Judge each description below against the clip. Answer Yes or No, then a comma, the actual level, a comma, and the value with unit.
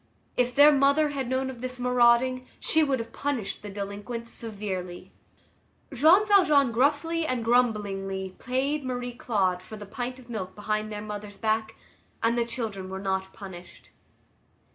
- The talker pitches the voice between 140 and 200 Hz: No, high, 235 Hz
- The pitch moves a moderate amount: Yes, average, 4.1 semitones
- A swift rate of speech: No, average, 155 wpm